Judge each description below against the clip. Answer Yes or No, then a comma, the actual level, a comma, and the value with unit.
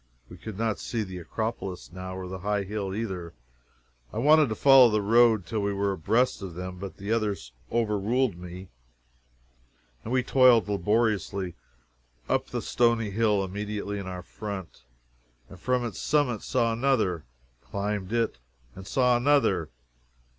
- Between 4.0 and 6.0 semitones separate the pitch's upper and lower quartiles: No, average, 3.6 semitones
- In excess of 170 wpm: No, average, 155 wpm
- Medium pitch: No, low, 105 Hz